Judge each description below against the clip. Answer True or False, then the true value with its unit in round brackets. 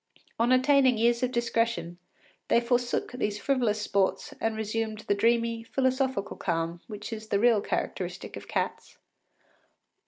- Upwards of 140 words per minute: False (135 wpm)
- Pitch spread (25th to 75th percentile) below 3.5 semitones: True (2.7 semitones)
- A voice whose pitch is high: True (230 Hz)